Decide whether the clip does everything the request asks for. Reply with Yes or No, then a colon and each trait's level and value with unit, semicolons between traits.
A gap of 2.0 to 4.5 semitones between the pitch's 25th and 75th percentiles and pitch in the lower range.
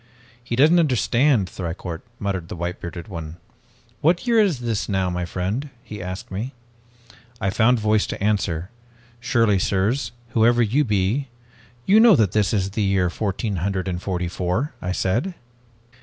No: average, 4.9 semitones; low, 105 Hz